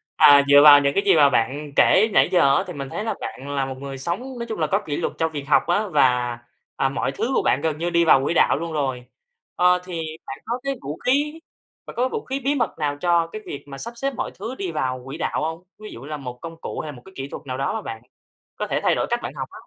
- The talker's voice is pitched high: No, medium, 160 Hz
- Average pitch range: No, wide, 6.4 semitones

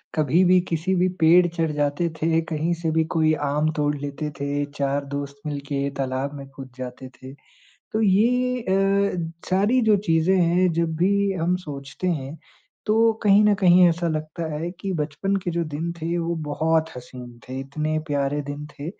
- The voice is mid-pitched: Yes, medium, 160 Hz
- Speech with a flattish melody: No, average, 4.0 semitones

